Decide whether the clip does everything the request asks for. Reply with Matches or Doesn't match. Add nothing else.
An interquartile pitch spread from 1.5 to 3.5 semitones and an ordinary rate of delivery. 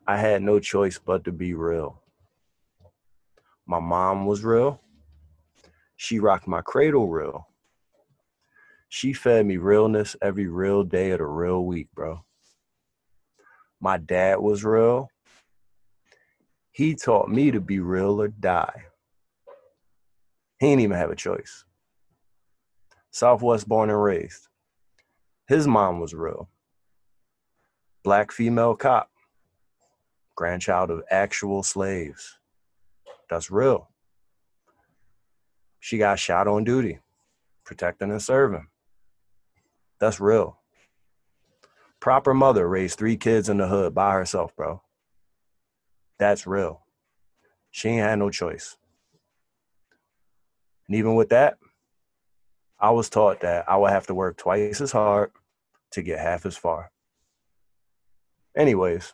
Doesn't match